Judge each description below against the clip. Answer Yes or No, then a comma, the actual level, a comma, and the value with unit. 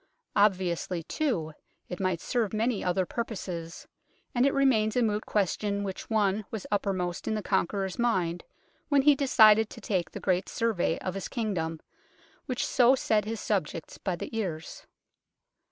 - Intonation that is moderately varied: Yes, average, 3.8 semitones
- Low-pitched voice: No, high, 205 Hz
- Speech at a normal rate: Yes, average, 155 wpm